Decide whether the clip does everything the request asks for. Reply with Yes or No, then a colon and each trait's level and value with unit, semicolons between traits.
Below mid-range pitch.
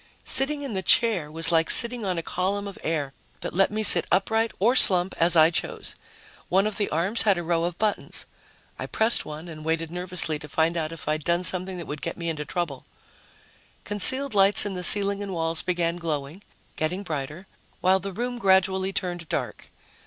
No: medium, 180 Hz